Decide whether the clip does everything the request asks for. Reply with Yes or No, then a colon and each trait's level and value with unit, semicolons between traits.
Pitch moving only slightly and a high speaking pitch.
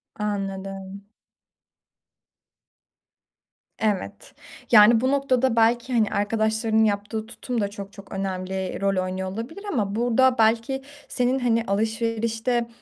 No: average, 3.0 semitones; high, 220 Hz